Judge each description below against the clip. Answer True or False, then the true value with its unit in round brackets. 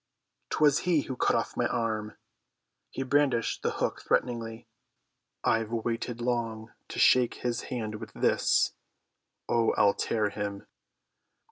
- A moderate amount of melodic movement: False (2.0 semitones)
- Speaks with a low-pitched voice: True (115 Hz)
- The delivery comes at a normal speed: False (125 wpm)